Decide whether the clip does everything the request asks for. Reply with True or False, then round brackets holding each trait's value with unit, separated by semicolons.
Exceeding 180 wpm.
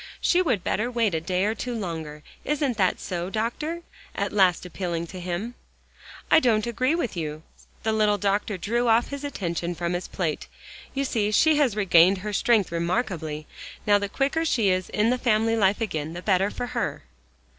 True (190 wpm)